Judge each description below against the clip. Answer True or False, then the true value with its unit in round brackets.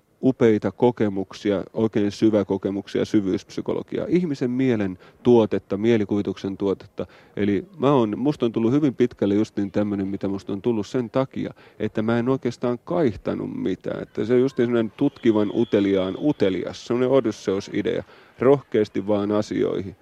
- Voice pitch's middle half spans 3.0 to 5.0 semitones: True (3.4 semitones)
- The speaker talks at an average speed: True (145 wpm)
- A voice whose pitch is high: False (110 Hz)